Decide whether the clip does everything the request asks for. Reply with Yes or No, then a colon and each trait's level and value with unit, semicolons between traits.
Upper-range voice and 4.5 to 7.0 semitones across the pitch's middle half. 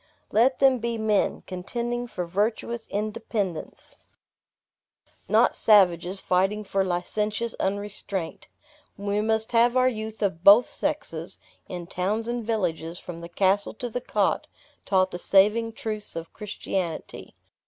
No: high, 210 Hz; average, 3.6 semitones